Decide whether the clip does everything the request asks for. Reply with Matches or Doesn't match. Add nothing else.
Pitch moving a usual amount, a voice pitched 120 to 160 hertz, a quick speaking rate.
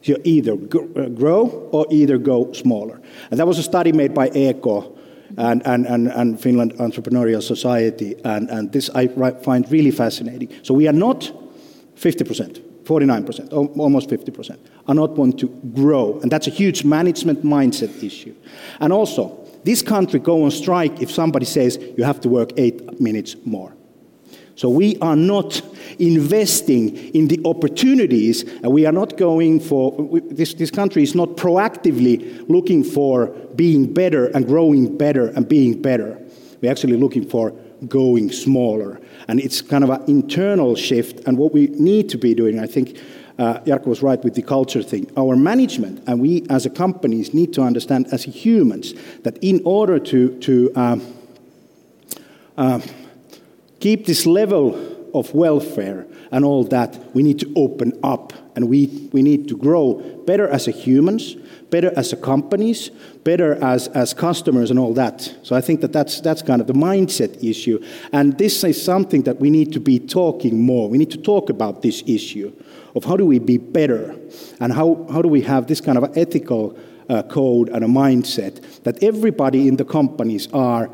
Matches